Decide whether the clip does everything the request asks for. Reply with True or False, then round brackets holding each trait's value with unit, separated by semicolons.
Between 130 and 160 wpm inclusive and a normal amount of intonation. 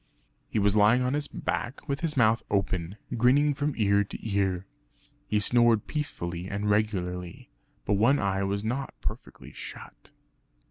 True (150 wpm; 4.3 semitones)